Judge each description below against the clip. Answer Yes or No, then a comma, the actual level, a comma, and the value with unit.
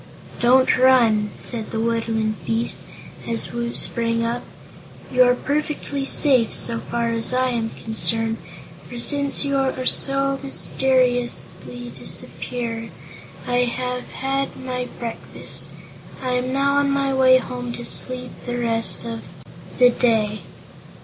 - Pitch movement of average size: No, narrow, 2.2 semitones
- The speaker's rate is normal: No, slow, 130 wpm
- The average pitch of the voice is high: Yes, high, 245 Hz